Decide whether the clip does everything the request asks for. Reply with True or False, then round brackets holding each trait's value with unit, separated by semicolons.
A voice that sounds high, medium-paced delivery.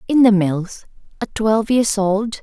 True (210 Hz; 150 wpm)